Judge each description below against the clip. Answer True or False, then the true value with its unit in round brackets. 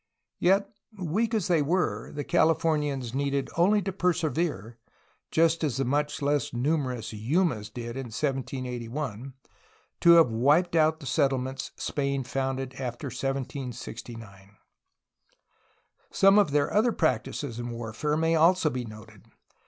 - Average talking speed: False (130 wpm)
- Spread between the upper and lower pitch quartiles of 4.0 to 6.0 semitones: True (5.0 semitones)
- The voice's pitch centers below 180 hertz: True (140 Hz)